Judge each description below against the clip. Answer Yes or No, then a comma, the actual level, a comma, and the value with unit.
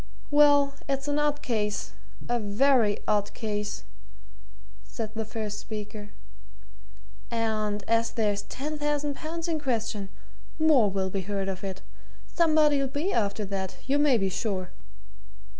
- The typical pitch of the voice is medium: No, high, 225 Hz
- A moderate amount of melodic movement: No, wide, 5.8 semitones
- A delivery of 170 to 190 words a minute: No, slow, 135 wpm